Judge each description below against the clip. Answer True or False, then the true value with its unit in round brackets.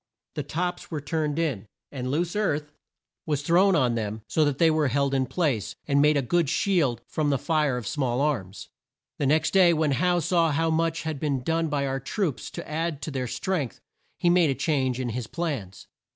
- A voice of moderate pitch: True (150 Hz)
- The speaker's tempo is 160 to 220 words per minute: True (205 wpm)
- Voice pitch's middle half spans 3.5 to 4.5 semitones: True (3.8 semitones)